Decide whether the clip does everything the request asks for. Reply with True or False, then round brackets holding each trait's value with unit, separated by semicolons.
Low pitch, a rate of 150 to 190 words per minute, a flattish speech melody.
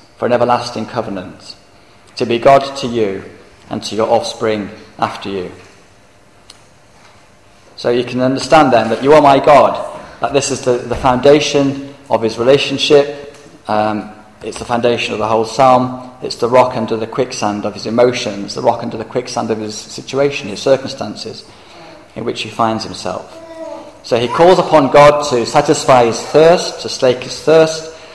False (120 Hz; 170 wpm; 4.2 semitones)